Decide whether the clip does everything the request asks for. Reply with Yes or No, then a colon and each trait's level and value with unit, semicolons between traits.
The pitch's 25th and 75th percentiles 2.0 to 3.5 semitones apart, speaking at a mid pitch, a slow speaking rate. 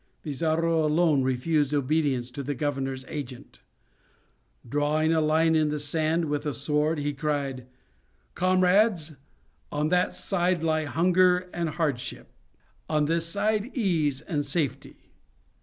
Yes: narrow, 2.6 semitones; medium, 155 Hz; slow, 125 wpm